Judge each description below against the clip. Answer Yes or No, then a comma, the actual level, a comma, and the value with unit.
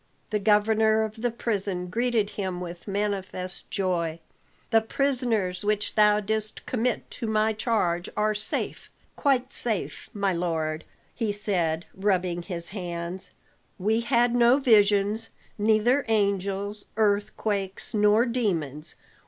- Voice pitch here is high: Yes, high, 210 Hz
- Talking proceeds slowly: Yes, slow, 120 wpm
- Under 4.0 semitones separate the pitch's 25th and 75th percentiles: Yes, average, 3.1 semitones